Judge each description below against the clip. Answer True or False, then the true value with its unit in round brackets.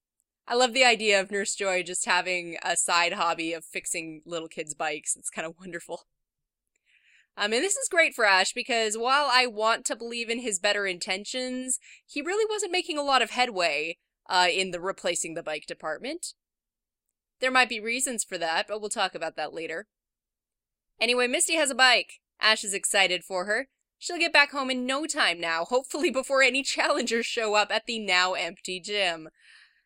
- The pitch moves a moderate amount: False (6.4 semitones)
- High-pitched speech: True (210 Hz)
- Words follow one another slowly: False (190 wpm)